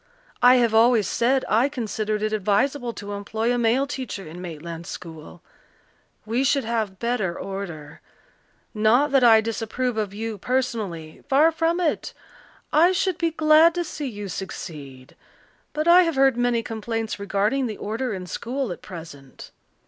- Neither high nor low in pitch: No, high, 225 Hz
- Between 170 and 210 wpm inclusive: No, average, 155 wpm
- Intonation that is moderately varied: Yes, average, 5.0 semitones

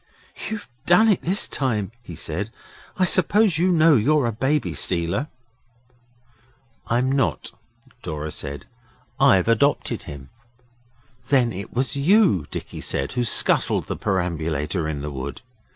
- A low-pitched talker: Yes, low, 115 Hz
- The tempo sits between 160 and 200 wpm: No, slow, 135 wpm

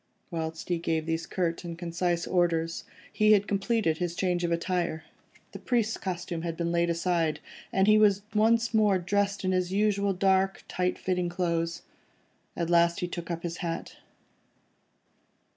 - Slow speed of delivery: No, average, 160 wpm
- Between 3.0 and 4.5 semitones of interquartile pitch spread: No, narrow, 2.6 semitones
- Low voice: No, medium, 175 Hz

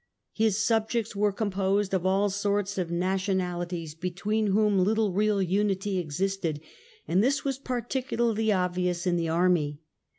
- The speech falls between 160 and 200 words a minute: No, slow, 135 wpm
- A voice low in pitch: No, high, 195 Hz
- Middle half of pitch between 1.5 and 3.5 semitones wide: Yes, average, 2.8 semitones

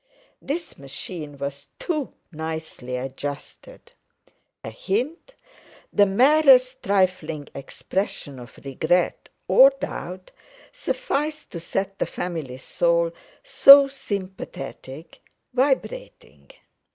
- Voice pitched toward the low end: No, medium, 185 Hz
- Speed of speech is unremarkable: No, slow, 85 wpm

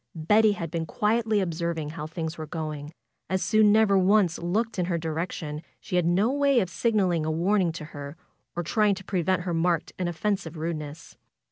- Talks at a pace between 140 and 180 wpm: No, average, 190 wpm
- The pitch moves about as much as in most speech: Yes, average, 4.1 semitones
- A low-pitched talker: No, medium, 175 Hz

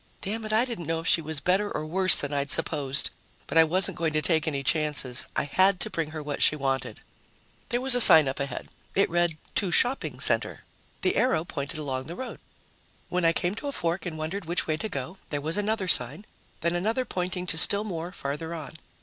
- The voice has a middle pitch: Yes, medium, 165 Hz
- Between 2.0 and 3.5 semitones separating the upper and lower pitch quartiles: No, average, 4.2 semitones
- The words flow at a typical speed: No, fast, 225 wpm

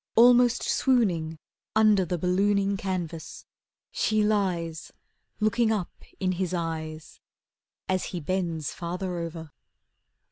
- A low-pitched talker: No, medium, 185 Hz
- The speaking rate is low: Yes, slow, 105 wpm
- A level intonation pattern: No, average, 3.8 semitones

